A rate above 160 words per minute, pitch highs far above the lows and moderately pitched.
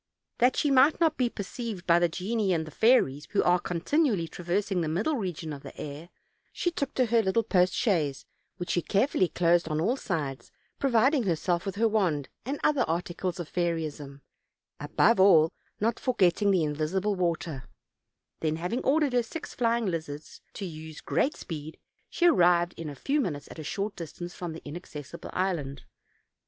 Yes: average, 185 wpm; wide, 6.1 semitones; medium, 180 Hz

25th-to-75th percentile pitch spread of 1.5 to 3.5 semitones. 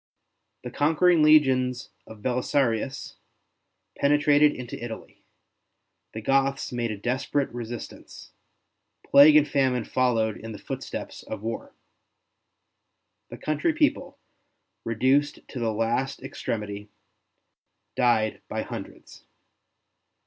No: average, 4.1 semitones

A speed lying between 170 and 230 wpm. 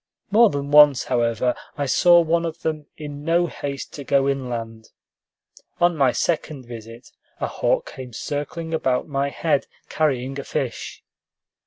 No: average, 150 wpm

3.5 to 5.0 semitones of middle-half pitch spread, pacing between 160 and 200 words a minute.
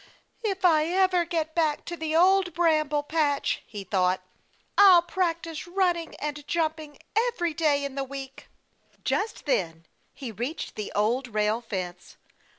No: average, 4.7 semitones; average, 145 wpm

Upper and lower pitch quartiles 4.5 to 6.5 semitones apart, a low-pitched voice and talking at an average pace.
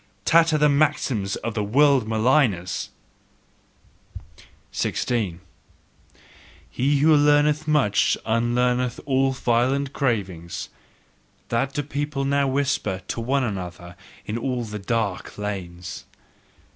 No: average, 5.2 semitones; low, 125 Hz; slow, 105 wpm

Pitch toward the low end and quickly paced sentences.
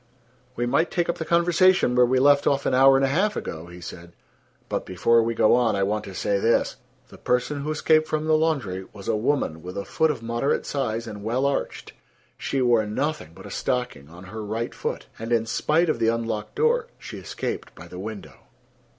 Yes: low, 120 Hz; fast, 220 wpm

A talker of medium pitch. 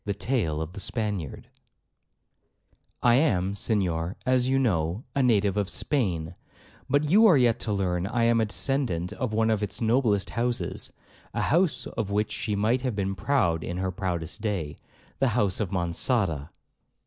No: low, 105 Hz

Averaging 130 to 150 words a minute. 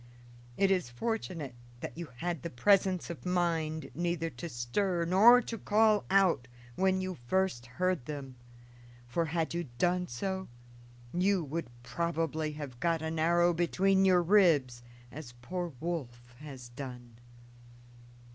Yes: slow, 135 wpm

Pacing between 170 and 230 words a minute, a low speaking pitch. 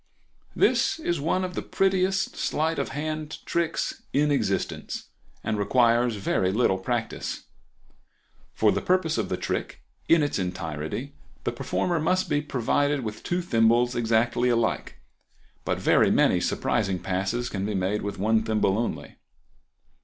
No: average, 145 wpm; low, 120 Hz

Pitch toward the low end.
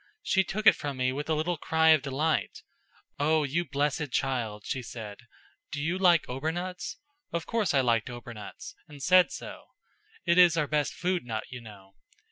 No: medium, 150 Hz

